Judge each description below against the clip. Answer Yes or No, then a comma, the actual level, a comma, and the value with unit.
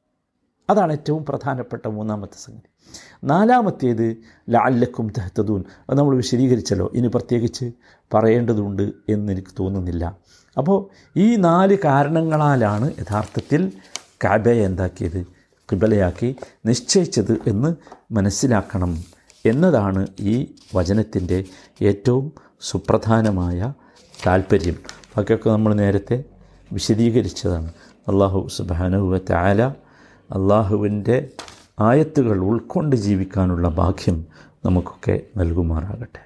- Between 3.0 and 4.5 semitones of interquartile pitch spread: No, average, 4.9 semitones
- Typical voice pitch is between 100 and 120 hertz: Yes, low, 110 Hz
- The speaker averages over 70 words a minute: Yes, average, 80 wpm